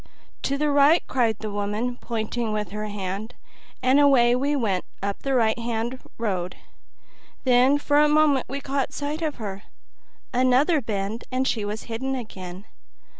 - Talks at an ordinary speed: Yes, average, 160 wpm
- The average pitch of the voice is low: No, high, 240 Hz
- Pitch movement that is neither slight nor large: Yes, average, 4.5 semitones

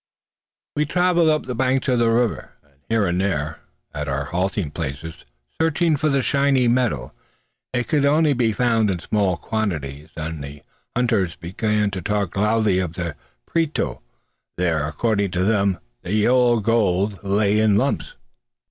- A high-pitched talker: No, low, 105 Hz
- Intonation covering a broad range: Yes, wide, 5.9 semitones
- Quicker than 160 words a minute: No, average, 155 wpm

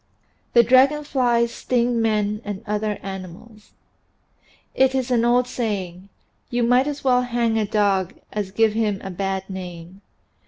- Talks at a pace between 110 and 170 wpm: Yes, average, 150 wpm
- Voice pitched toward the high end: Yes, high, 220 Hz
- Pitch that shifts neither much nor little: Yes, average, 3.8 semitones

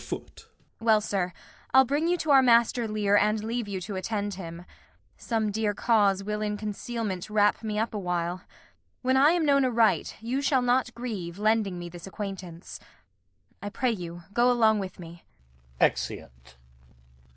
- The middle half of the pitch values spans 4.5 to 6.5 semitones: No, average, 4.0 semitones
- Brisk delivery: No, average, 160 wpm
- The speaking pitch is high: Yes, high, 210 Hz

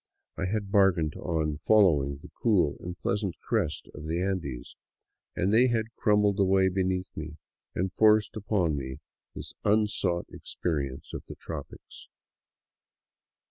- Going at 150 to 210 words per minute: No, average, 140 wpm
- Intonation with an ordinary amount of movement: Yes, average, 4.8 semitones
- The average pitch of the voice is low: Yes, very low, 95 Hz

